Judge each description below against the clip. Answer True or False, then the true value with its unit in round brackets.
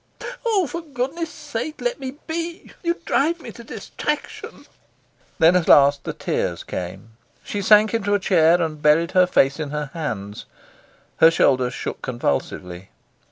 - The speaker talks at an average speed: True (155 wpm)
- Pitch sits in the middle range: True (180 Hz)